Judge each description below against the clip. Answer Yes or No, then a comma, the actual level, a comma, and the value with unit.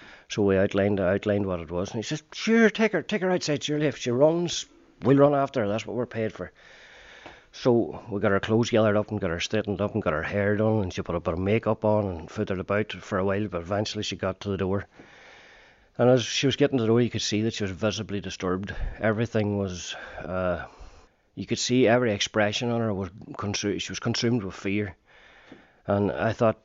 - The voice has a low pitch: Yes, low, 105 Hz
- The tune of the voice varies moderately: Yes, average, 3.2 semitones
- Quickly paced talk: Yes, fast, 230 wpm